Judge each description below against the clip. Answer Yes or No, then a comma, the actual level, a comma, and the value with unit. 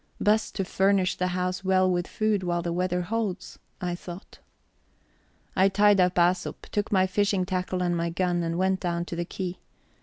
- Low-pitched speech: No, medium, 185 Hz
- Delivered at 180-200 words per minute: Yes, average, 185 wpm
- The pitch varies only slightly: Yes, narrow, 1.6 semitones